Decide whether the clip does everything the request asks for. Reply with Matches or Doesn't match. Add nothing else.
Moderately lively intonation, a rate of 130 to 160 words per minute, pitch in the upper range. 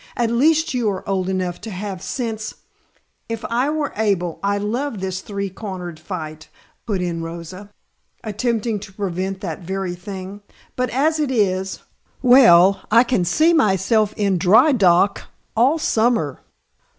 Matches